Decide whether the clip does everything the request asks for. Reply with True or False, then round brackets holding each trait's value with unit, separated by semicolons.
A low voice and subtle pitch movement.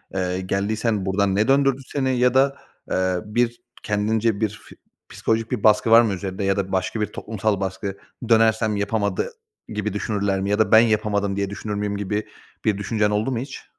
True (105 Hz; 2.1 semitones)